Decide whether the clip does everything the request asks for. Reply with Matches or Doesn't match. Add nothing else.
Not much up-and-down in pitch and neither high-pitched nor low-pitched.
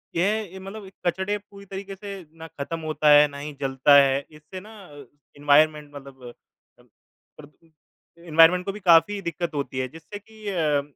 Doesn't match